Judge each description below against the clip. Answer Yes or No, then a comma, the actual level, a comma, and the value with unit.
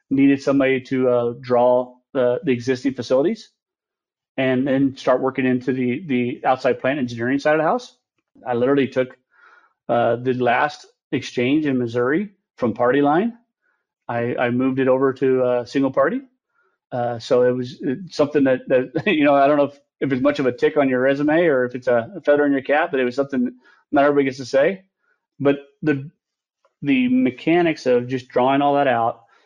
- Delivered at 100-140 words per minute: No, average, 190 wpm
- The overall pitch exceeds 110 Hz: Yes, low, 135 Hz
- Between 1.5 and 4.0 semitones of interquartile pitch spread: Yes, average, 2.8 semitones